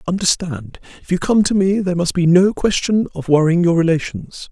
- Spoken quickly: Yes, fast, 210 wpm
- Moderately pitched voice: Yes, medium, 175 Hz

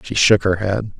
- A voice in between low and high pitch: No, low, 100 Hz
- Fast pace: Yes, fast, 240 wpm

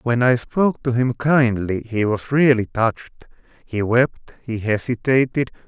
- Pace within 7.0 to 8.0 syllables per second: No, 4.5 syllables/s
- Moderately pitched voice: No, low, 120 Hz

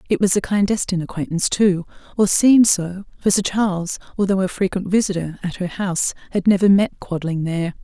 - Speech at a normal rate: Yes, average, 185 wpm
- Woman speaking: Yes, female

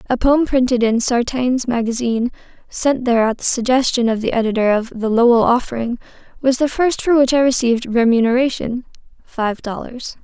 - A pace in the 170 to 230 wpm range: No, average, 160 wpm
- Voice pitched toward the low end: No, high, 245 Hz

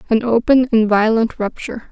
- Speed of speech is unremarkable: Yes, average, 155 wpm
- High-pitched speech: Yes, high, 225 Hz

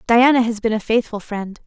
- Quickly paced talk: Yes, fast, 215 wpm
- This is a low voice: No, high, 225 Hz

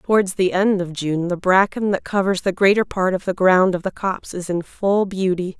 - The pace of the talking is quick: Yes, fast, 235 wpm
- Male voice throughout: No, female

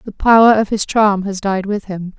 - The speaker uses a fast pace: Yes, fast, 245 wpm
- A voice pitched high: Yes, high, 200 Hz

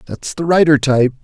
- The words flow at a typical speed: Yes, average, 195 wpm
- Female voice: No, male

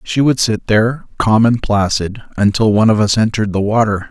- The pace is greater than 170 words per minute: Yes, fast, 205 wpm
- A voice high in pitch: No, low, 110 Hz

